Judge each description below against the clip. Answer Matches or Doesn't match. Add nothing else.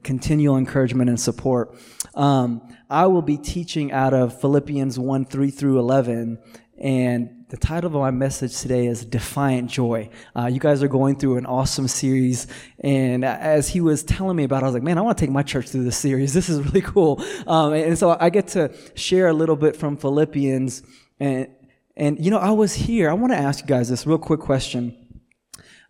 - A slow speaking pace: Doesn't match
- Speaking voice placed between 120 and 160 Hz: Matches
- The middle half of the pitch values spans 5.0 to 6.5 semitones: Doesn't match